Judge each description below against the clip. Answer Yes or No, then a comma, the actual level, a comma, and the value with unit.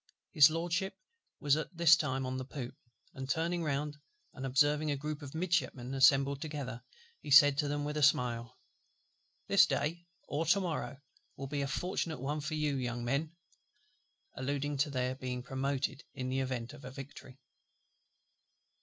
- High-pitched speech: No, medium, 140 Hz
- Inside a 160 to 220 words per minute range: Yes, average, 165 wpm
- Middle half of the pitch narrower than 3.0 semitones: Yes, narrow, 2.6 semitones